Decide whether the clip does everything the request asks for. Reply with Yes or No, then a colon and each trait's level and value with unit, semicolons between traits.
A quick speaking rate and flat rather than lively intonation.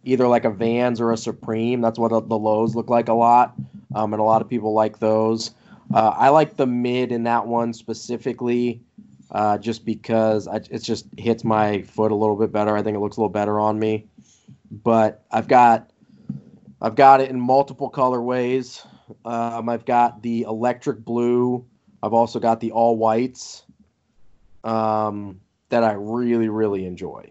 No: average, 180 wpm; narrow, 1.8 semitones